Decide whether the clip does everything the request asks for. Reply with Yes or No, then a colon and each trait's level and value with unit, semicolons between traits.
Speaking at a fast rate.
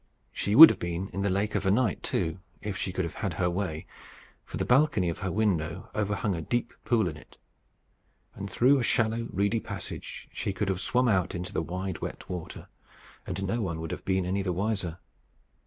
Yes: fast, 210 wpm